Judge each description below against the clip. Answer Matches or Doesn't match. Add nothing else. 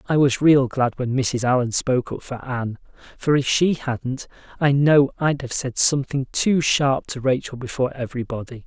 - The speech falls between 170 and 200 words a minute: Matches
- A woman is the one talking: Doesn't match